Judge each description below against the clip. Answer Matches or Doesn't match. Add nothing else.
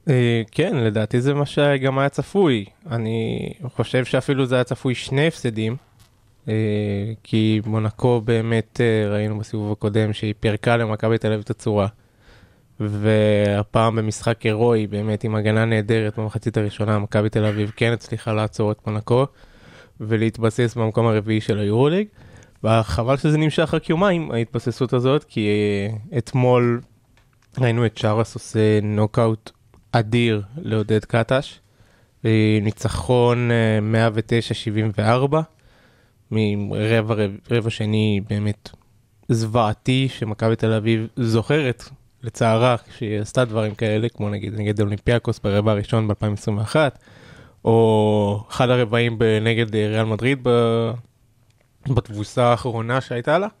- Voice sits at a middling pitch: Doesn't match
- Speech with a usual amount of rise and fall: Doesn't match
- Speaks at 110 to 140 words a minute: Matches